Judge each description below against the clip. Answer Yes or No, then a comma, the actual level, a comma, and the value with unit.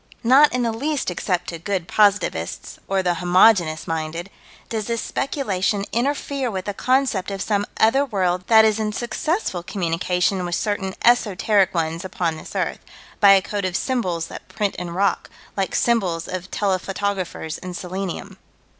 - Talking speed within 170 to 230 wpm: No, average, 160 wpm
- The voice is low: No, high, 195 Hz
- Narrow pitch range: No, average, 3.7 semitones